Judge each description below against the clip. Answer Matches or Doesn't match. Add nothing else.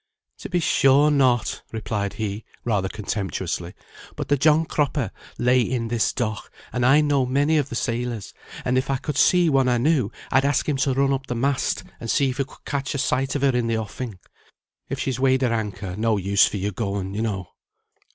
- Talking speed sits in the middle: Doesn't match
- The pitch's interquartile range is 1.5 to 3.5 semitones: Doesn't match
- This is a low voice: Matches